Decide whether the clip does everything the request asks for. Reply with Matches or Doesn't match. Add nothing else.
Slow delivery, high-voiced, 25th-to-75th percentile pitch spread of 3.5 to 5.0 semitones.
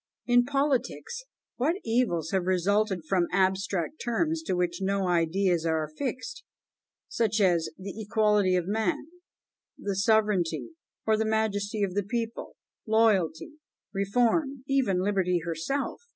Matches